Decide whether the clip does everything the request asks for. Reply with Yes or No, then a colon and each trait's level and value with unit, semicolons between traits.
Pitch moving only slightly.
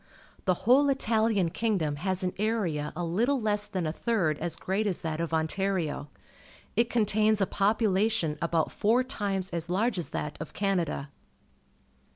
No: average, 4.7 semitones